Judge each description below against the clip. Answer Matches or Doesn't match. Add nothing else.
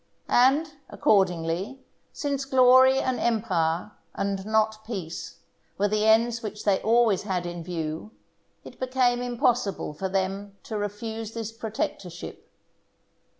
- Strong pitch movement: Doesn't match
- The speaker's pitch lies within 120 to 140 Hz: Doesn't match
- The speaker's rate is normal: Doesn't match